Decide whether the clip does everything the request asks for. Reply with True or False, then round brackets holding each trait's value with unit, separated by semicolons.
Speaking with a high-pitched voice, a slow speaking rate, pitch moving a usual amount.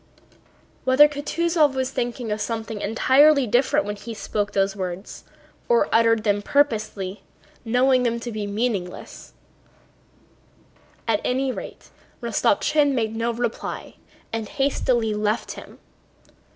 True (230 Hz; 120 wpm; 3.8 semitones)